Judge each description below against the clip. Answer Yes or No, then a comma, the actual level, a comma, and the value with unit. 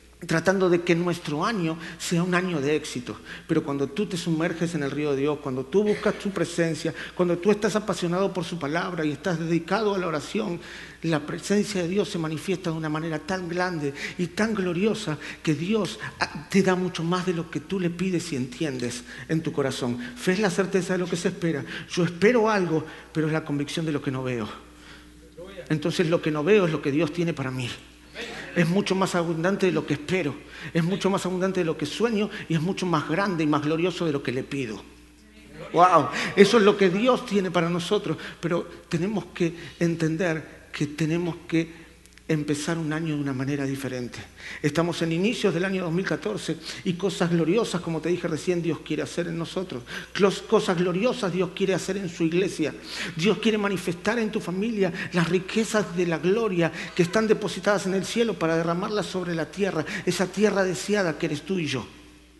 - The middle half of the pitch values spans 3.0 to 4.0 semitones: Yes, average, 3.4 semitones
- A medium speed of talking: No, fast, 200 wpm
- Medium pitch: Yes, medium, 175 Hz